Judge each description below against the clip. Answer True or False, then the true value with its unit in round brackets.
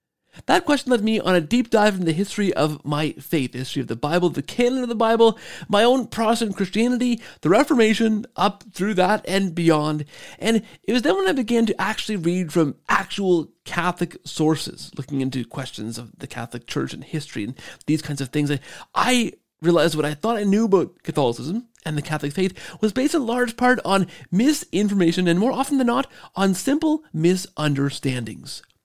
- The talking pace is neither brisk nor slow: True (190 wpm)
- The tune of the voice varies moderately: False (6.8 semitones)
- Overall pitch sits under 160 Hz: False (190 Hz)